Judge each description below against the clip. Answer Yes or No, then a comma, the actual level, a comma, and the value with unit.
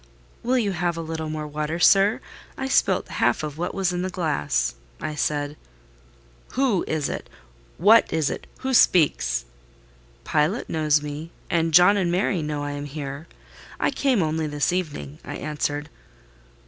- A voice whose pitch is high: No, medium, 160 Hz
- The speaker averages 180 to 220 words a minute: No, average, 160 wpm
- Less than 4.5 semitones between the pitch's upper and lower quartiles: Yes, average, 3.6 semitones